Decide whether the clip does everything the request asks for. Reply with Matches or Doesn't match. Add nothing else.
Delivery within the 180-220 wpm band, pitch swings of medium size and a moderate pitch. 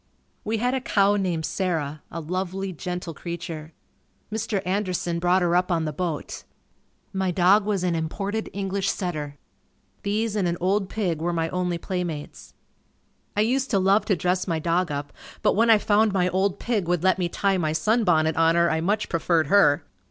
Matches